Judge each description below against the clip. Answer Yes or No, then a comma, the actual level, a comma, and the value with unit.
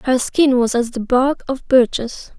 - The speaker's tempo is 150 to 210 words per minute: Yes, average, 200 wpm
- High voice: Yes, very high, 250 Hz